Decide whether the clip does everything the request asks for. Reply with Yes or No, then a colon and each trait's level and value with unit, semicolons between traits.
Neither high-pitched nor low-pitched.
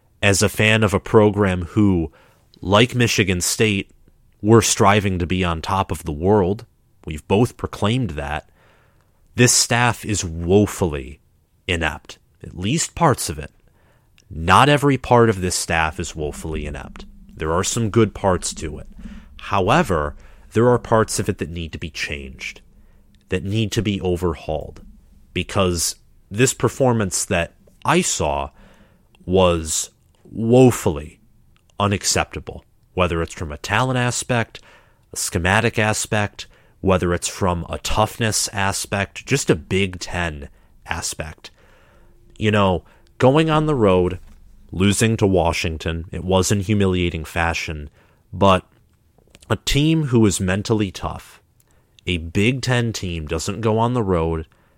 No: very low, 95 Hz